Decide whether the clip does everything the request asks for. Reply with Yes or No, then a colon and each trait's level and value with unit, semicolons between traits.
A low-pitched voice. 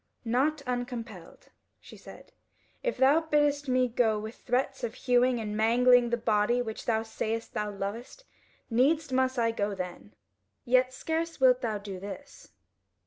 No: high, 245 Hz